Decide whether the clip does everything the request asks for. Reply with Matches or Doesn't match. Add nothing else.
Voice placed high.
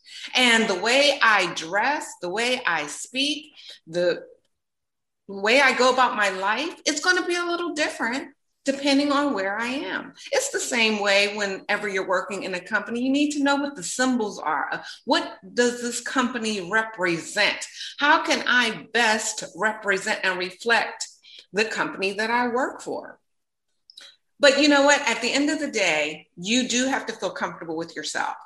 Matches